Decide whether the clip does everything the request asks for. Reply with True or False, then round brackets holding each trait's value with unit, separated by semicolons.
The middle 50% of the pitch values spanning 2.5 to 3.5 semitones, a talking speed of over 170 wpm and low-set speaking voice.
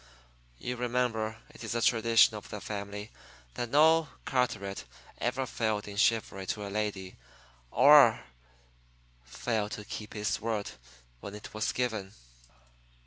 False (2.8 semitones; 135 wpm; 110 Hz)